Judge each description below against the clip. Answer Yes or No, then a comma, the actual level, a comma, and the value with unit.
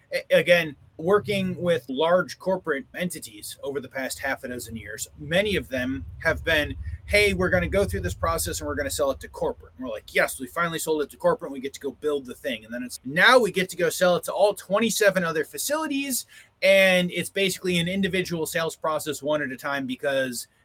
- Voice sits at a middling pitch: Yes, medium, 170 Hz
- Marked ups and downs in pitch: Yes, wide, 6.2 semitones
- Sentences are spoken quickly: Yes, fast, 230 wpm